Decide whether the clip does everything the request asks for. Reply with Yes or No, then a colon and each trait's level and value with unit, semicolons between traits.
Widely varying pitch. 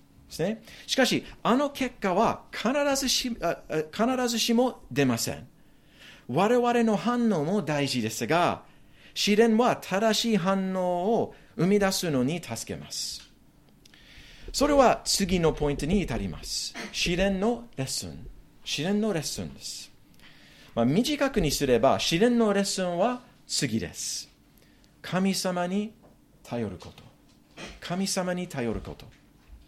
Yes: wide, 8.2 semitones